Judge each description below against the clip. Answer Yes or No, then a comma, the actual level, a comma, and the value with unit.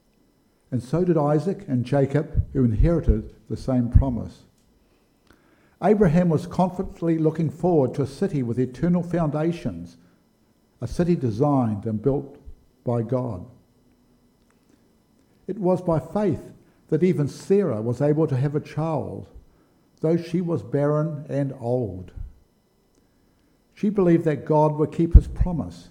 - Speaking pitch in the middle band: Yes, medium, 145 Hz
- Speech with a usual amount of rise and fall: No, wide, 5.7 semitones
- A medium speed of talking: No, slow, 130 wpm